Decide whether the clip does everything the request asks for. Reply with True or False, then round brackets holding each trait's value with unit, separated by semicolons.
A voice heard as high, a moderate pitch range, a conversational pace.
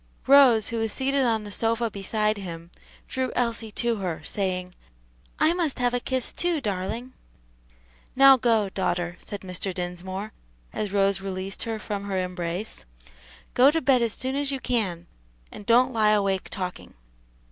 True (215 Hz; 4.6 semitones; 160 wpm)